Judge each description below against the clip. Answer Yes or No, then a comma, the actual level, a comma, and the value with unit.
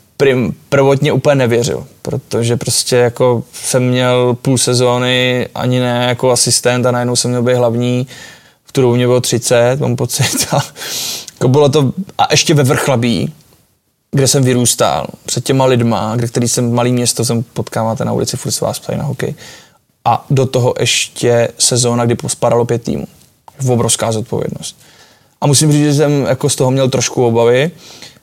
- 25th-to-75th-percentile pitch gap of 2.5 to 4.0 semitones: No, narrow, 2.0 semitones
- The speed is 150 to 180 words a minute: Yes, fast, 170 wpm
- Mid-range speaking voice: No, low, 125 Hz